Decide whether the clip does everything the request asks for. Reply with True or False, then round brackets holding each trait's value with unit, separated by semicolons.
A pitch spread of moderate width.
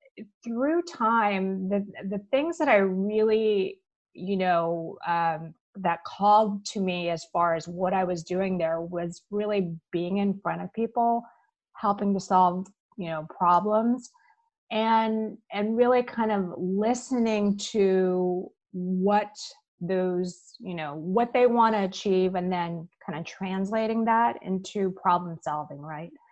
True (3.7 semitones)